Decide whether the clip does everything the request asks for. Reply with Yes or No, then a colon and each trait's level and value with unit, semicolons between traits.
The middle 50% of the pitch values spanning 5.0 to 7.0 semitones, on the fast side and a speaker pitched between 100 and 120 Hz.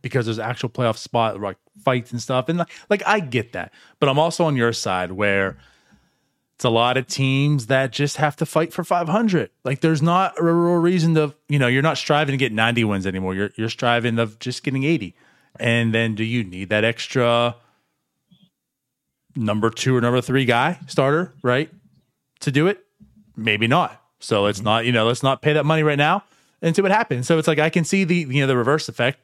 No: wide, 5.5 semitones; fast, 220 wpm; low, 135 Hz